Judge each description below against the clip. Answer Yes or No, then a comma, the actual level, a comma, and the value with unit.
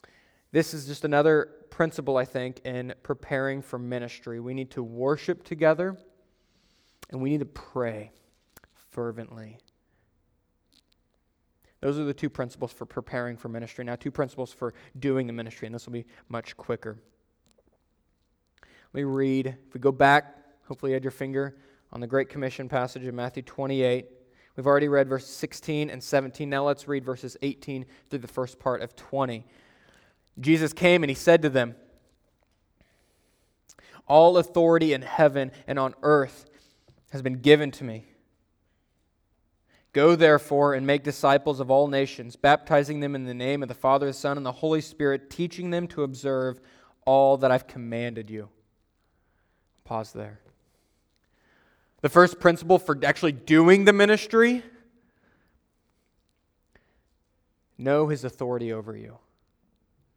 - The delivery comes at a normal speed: Yes, average, 145 wpm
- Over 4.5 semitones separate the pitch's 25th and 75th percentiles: No, average, 3.5 semitones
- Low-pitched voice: Yes, low, 130 Hz